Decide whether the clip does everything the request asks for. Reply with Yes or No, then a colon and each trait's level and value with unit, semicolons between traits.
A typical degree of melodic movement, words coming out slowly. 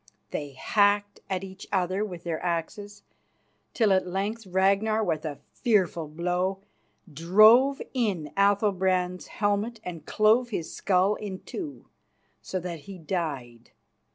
Yes: average, 3.1 semitones; slow, 125 wpm